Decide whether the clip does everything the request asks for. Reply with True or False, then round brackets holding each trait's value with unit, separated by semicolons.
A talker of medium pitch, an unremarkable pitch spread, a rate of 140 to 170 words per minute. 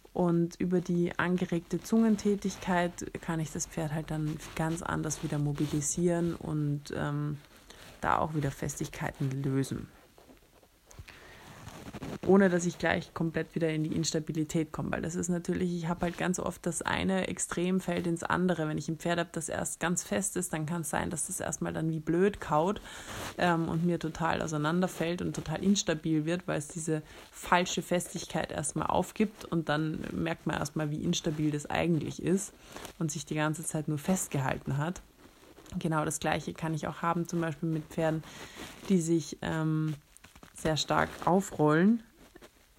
False (165 Hz; 2.2 semitones; 165 wpm)